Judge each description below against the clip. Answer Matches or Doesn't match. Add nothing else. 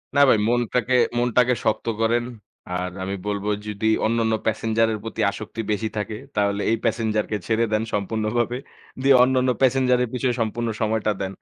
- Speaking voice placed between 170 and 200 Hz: Doesn't match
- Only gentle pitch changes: Matches